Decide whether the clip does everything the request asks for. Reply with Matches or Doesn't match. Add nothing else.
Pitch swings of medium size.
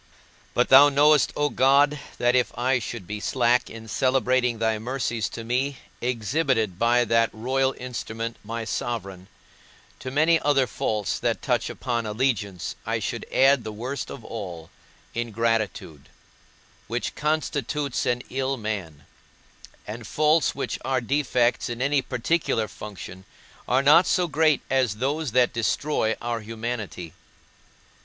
Matches